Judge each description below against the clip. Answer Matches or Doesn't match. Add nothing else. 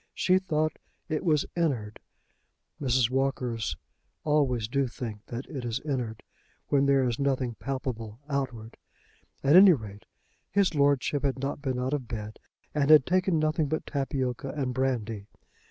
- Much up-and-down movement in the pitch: Doesn't match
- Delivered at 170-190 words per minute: Doesn't match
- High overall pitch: Doesn't match